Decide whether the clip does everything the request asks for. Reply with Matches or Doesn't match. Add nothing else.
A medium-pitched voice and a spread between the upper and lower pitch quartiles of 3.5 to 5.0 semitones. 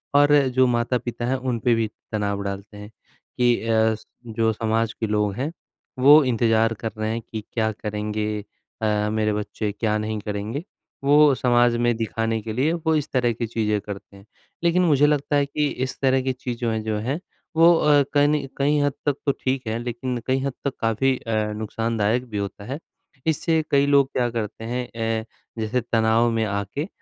Doesn't match